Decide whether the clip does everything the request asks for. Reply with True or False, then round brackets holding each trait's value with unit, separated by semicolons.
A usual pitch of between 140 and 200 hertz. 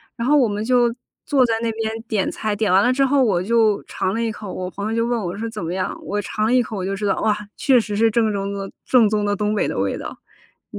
False (215 Hz)